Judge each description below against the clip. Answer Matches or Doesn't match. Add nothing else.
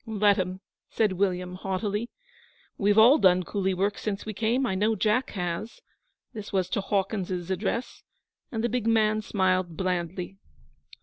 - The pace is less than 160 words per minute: Matches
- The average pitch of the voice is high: Matches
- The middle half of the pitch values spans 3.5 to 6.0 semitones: Doesn't match